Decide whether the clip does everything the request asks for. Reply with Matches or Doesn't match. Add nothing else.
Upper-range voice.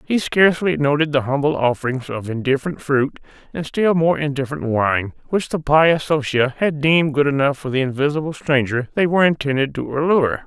Doesn't match